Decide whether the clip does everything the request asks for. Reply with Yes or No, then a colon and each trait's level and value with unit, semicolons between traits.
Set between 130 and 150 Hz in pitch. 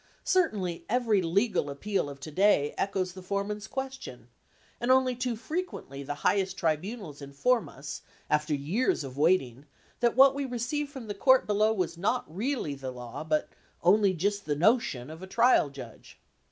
No: high, 195 Hz